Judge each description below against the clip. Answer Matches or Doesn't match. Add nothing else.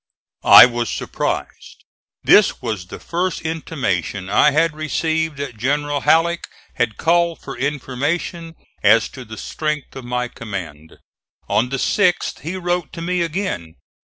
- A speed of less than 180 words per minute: Matches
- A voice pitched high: Doesn't match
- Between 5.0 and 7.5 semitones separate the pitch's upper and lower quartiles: Matches